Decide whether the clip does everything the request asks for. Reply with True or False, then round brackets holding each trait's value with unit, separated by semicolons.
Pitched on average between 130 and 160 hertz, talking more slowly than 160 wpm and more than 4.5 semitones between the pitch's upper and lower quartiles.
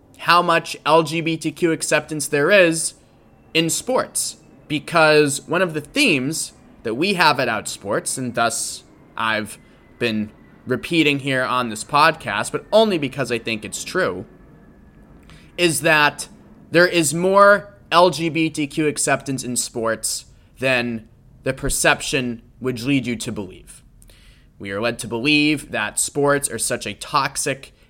True (140 Hz; 135 wpm; 5.1 semitones)